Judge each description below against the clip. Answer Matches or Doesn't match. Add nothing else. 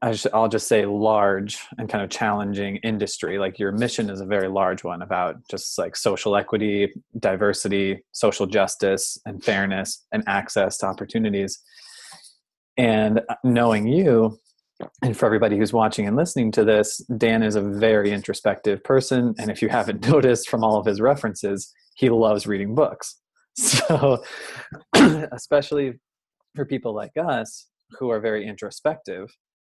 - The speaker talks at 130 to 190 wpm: Matches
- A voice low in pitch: Matches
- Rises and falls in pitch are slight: Matches